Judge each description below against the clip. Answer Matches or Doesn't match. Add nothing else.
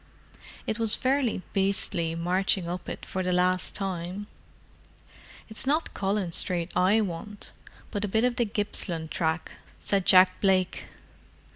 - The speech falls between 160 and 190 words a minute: Doesn't match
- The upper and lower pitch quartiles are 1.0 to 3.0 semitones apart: Matches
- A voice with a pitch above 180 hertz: Matches